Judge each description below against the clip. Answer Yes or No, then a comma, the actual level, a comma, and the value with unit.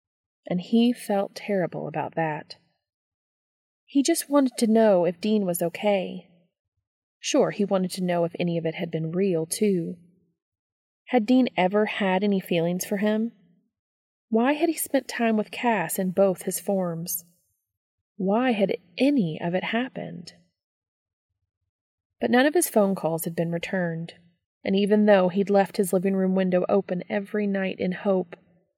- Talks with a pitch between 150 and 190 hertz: Yes, medium, 185 Hz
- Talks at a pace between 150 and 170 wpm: Yes, average, 160 wpm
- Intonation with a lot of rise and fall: No, average, 4.0 semitones